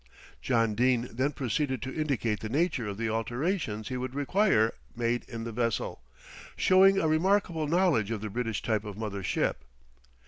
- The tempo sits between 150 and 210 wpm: Yes, average, 170 wpm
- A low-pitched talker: Yes, low, 125 Hz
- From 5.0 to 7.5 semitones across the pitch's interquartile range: Yes, wide, 5.6 semitones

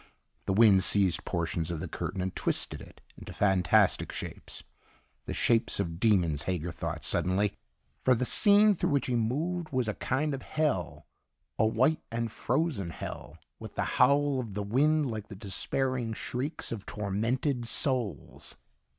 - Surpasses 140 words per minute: Yes, average, 160 wpm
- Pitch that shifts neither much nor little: No, wide, 5.8 semitones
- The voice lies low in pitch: Yes, low, 115 Hz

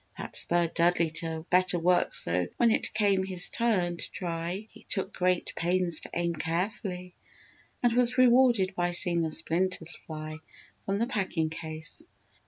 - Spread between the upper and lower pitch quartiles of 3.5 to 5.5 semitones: No, average, 2.8 semitones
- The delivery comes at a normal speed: Yes, average, 160 wpm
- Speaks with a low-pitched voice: No, medium, 180 Hz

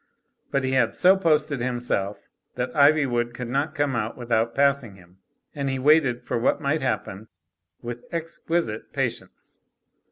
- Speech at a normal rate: Yes, average, 150 wpm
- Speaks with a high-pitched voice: No, low, 130 Hz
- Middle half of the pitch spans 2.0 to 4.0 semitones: Yes, average, 3.5 semitones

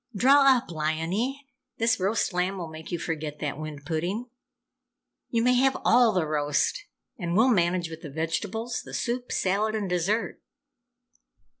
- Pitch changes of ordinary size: No, wide, 6.4 semitones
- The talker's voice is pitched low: No, medium, 185 Hz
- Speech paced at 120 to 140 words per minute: No, average, 155 wpm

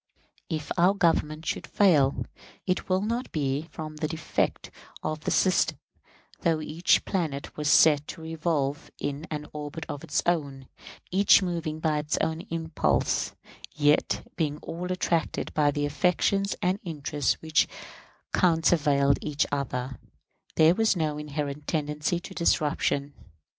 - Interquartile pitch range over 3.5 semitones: No, narrow, 2.6 semitones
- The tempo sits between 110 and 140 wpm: Yes, slow, 135 wpm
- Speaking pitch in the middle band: Yes, medium, 155 Hz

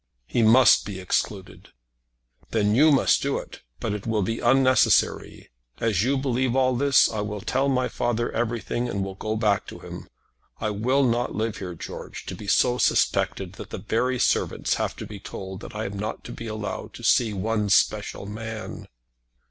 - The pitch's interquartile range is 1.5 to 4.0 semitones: Yes, average, 3.2 semitones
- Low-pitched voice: Yes, low, 115 Hz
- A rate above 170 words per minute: Yes, average, 190 wpm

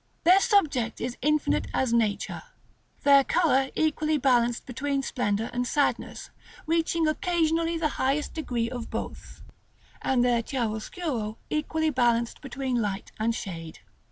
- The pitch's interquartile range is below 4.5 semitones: No, average, 4.8 semitones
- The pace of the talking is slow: Yes, slow, 130 wpm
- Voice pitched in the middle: No, very high, 265 Hz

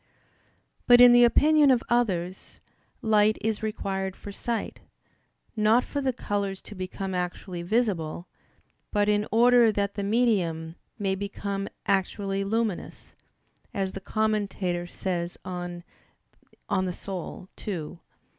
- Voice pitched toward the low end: No, high, 200 Hz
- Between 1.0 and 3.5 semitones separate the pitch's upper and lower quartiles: Yes, average, 3.1 semitones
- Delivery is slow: Yes, slow, 120 wpm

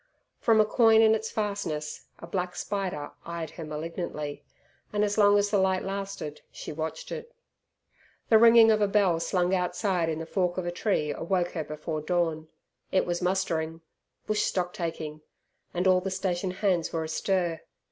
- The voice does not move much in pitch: No, average, 3.8 semitones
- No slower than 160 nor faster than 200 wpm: Yes, average, 165 wpm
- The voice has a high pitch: No, medium, 180 Hz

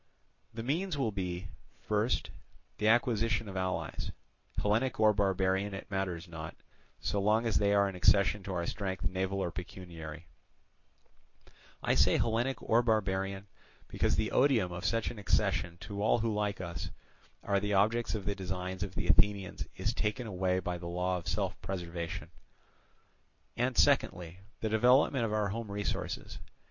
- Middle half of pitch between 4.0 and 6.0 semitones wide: No, average, 3.0 semitones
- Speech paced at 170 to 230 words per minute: No, average, 155 wpm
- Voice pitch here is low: Yes, low, 100 Hz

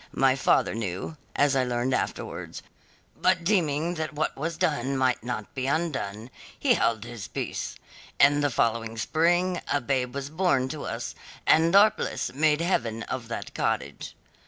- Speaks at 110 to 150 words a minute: No, average, 160 wpm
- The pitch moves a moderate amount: Yes, average, 4.8 semitones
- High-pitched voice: No, low, 135 Hz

